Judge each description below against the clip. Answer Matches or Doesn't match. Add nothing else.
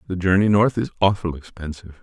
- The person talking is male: Matches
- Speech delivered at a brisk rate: Doesn't match